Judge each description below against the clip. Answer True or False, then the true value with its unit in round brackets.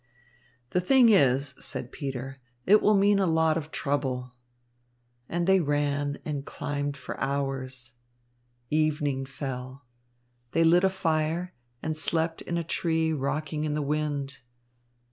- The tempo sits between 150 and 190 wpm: False (135 wpm)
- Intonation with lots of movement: False (3.0 semitones)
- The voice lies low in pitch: False (150 Hz)